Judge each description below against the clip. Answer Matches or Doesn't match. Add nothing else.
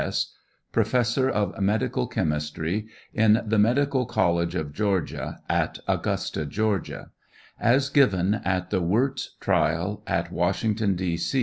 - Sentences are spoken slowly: Matches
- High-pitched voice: Doesn't match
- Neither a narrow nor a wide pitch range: Matches